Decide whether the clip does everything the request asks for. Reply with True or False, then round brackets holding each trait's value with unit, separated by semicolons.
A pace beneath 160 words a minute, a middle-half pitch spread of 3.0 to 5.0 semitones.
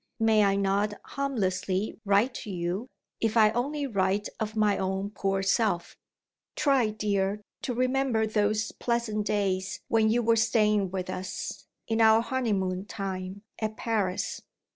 False (140 wpm; 2.6 semitones)